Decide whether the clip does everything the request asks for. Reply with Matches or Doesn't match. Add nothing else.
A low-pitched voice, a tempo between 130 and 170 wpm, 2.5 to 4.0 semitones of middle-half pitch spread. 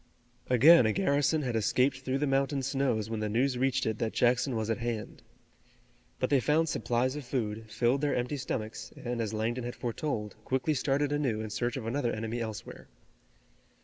Doesn't match